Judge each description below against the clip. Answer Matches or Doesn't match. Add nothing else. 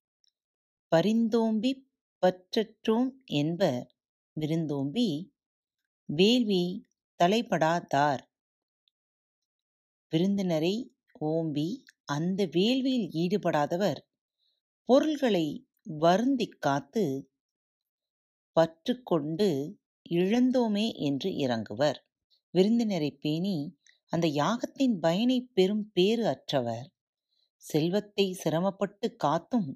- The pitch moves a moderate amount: Doesn't match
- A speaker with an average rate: Doesn't match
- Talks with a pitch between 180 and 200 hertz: Matches